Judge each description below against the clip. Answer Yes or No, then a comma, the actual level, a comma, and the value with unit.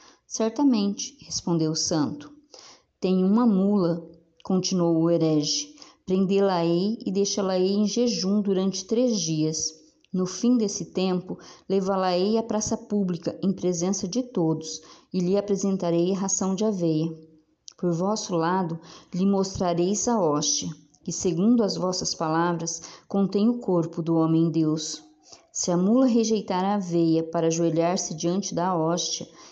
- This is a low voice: No, medium, 185 Hz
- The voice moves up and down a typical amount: Yes, average, 3.4 semitones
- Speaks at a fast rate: No, average, 135 wpm